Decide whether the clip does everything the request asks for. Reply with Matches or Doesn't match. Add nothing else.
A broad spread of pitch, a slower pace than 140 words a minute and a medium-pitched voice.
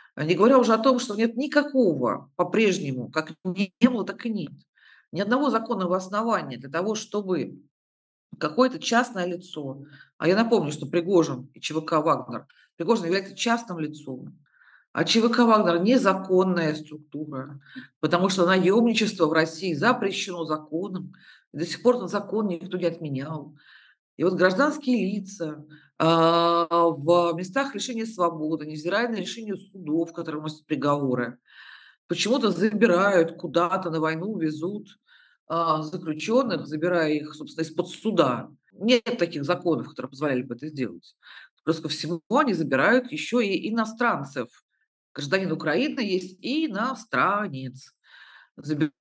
Matches